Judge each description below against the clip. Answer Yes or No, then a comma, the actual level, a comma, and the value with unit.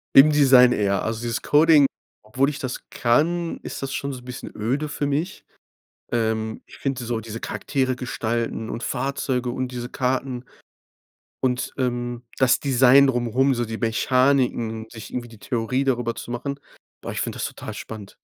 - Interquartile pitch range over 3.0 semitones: No, average, 2.7 semitones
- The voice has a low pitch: Yes, low, 125 Hz